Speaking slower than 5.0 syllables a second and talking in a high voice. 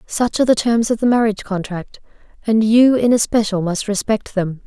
No: 5.4 syllables/s; high, 215 Hz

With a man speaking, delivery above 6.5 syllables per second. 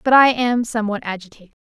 No: female; 7.0 syllables/s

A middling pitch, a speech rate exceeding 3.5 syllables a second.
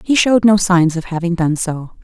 Yes: medium, 180 Hz; 5.3 syllables/s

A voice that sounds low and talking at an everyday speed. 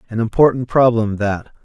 Yes: low, 115 Hz; average, 145 wpm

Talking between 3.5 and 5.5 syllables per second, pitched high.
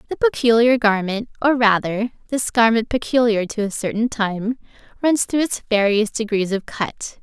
Yes: 4.7 syllables/s; high, 225 Hz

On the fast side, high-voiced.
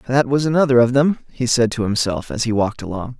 No: fast, 245 wpm; low, 125 Hz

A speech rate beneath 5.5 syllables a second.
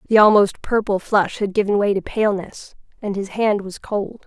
Yes: 5.0 syllables/s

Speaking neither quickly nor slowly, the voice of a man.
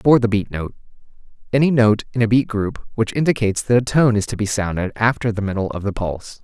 No: fast, 235 wpm; male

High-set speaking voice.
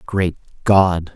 No: very low, 90 Hz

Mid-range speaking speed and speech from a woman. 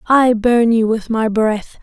Yes: average, 195 wpm; female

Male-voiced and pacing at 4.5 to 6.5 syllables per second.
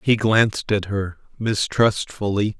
No: male; 3.9 syllables/s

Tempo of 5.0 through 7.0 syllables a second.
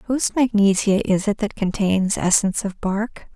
No: 4.8 syllables/s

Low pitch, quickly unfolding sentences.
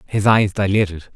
No: low, 100 Hz; average, 155 wpm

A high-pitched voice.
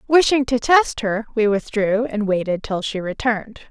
Yes: high, 225 Hz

